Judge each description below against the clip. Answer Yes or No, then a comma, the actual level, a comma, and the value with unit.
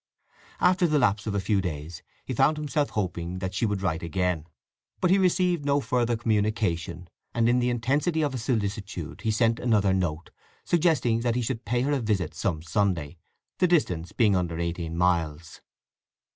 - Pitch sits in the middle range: No, low, 105 Hz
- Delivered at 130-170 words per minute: No, average, 180 wpm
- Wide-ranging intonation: Yes, wide, 6.3 semitones